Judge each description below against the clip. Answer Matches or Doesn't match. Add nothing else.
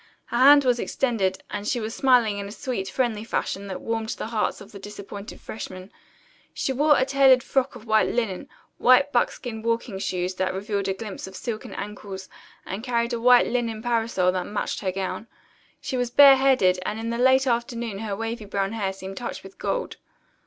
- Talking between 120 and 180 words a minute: Doesn't match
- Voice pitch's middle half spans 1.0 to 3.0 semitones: Doesn't match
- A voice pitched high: Matches